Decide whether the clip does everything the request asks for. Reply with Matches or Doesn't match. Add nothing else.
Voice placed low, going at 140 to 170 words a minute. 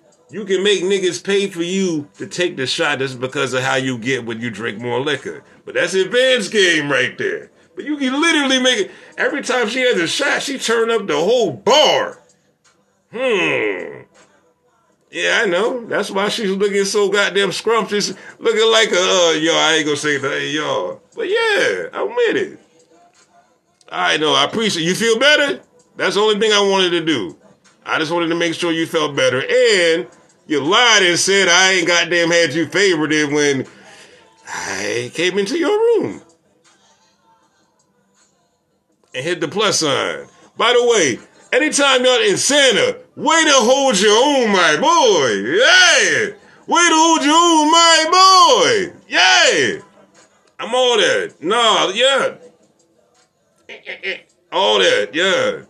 Doesn't match